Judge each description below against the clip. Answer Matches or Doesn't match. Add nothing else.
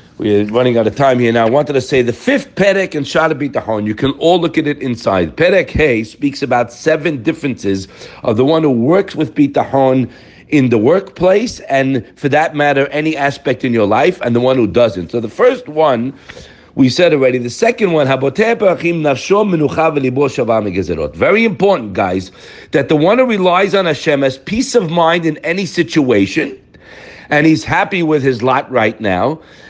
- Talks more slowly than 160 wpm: Doesn't match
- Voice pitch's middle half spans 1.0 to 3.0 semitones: Doesn't match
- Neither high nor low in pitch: Matches